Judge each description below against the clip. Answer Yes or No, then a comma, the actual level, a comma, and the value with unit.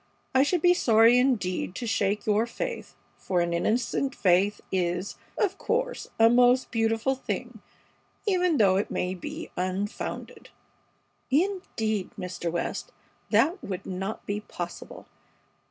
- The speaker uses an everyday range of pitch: No, wide, 6.0 semitones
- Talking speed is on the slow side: Yes, slow, 130 wpm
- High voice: Yes, high, 220 Hz